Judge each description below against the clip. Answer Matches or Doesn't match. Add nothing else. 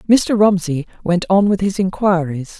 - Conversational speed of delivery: Matches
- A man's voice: Doesn't match